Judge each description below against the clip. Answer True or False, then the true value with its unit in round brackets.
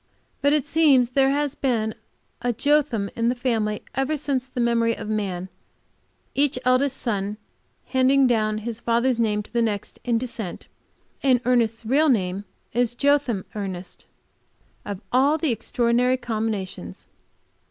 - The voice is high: True (240 Hz)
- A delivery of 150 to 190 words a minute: False (140 wpm)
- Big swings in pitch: False (3.6 semitones)